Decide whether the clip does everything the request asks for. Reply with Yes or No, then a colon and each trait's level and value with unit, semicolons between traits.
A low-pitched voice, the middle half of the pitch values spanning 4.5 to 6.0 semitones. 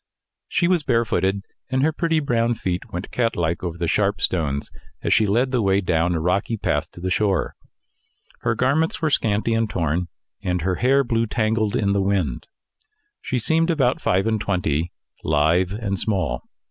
Yes: low, 100 Hz; average, 5.0 semitones